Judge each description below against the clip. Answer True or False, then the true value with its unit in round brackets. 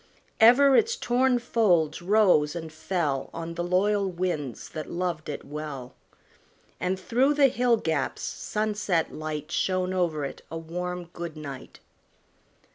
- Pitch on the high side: False (175 Hz)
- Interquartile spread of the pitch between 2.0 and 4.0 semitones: False (5.2 semitones)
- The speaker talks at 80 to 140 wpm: True (135 wpm)